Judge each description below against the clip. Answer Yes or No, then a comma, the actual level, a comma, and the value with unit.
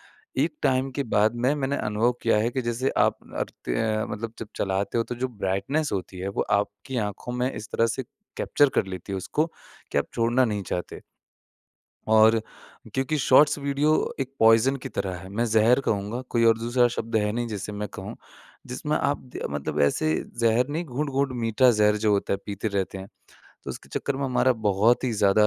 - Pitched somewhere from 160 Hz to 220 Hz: No, low, 115 Hz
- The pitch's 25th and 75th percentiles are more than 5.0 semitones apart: No, average, 3.8 semitones